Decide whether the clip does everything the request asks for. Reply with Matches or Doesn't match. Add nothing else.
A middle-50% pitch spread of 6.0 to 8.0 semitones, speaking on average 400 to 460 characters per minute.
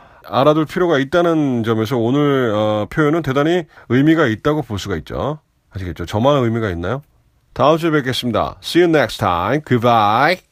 Doesn't match